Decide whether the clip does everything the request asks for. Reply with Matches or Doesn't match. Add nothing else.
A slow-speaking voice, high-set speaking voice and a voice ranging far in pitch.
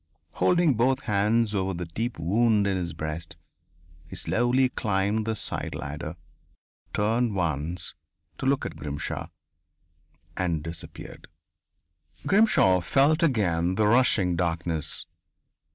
Doesn't match